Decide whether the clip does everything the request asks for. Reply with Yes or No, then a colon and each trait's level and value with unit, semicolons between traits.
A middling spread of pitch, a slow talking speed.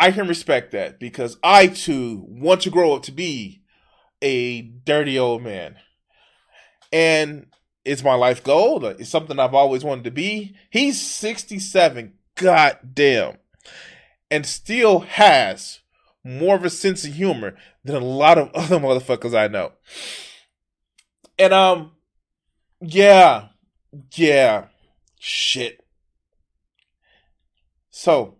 No: wide, 7.0 semitones; slow, 115 wpm